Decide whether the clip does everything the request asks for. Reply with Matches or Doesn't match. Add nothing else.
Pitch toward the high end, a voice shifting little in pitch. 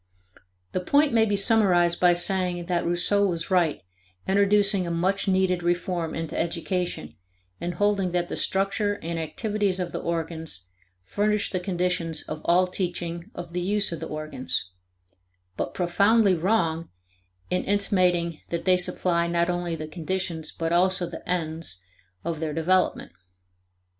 Doesn't match